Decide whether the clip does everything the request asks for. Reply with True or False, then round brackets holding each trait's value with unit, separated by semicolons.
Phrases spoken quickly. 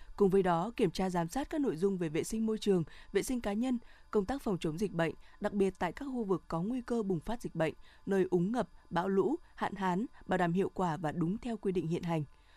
True (265 wpm)